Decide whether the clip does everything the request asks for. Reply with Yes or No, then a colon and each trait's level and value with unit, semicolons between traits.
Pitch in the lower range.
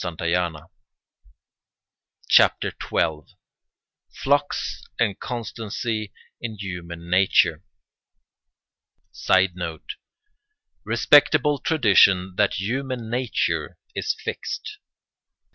Yes: low, 105 Hz